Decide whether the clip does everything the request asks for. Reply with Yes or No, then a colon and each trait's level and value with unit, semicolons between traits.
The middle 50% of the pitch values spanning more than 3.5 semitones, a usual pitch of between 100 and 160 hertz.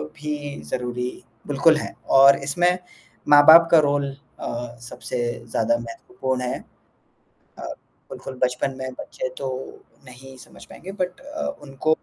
Yes: average, 3.9 semitones; medium, 140 Hz